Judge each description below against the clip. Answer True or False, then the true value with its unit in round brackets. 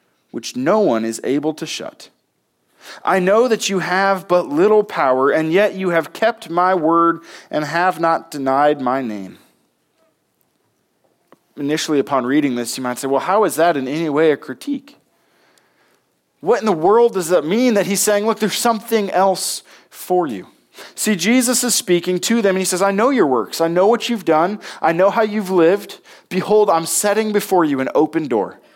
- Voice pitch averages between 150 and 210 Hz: True (185 Hz)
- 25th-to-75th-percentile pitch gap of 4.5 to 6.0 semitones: True (5.3 semitones)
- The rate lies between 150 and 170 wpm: False (190 wpm)